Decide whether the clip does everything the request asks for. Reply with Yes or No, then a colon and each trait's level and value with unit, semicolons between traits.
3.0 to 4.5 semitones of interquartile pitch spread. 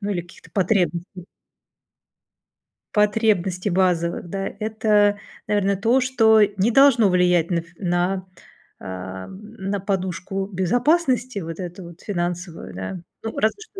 Yes: average, 3.5 semitones